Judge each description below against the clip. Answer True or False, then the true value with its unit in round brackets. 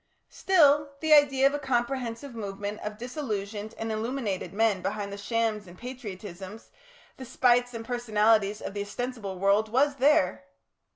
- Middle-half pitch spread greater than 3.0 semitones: True (4.1 semitones)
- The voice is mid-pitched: False (225 Hz)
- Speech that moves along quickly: False (150 wpm)